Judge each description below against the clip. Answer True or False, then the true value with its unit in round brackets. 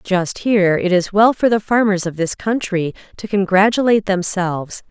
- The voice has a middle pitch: False (195 Hz)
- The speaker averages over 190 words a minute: False (170 wpm)